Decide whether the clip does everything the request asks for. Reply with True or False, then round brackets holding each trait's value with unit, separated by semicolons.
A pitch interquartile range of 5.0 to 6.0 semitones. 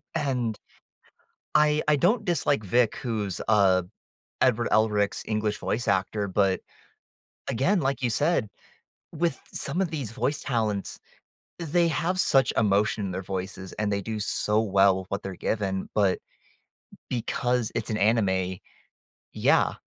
True (5.5 semitones)